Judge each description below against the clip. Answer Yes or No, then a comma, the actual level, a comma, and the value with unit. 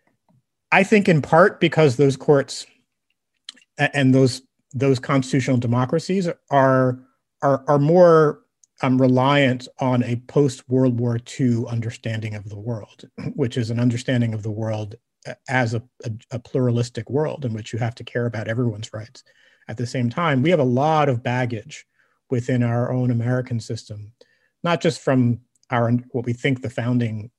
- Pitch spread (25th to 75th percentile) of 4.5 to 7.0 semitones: No, average, 2.7 semitones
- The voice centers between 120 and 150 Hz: Yes, low, 125 Hz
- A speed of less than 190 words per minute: Yes, average, 160 wpm